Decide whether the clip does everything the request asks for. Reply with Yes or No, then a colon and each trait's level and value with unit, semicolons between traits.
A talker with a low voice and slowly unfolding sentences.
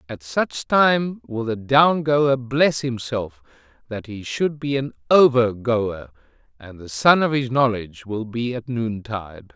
No: low, 120 Hz; average, 165 wpm